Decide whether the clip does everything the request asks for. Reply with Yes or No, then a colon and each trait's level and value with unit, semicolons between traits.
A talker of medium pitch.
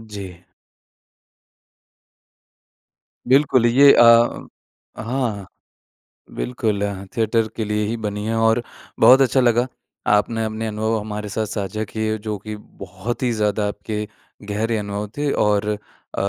No: low, 110 Hz